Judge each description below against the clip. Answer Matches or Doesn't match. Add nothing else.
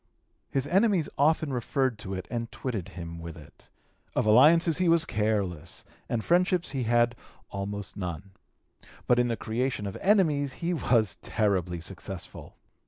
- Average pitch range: Doesn't match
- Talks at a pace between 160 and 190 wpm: Doesn't match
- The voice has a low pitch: Matches